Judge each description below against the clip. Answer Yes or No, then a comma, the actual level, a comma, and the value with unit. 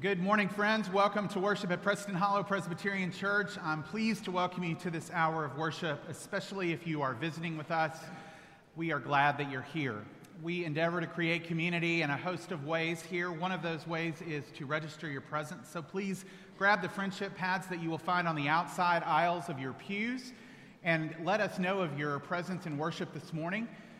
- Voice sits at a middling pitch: Yes, medium, 170 Hz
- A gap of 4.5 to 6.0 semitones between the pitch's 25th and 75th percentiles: No, average, 3.2 semitones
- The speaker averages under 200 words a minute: No, fast, 205 wpm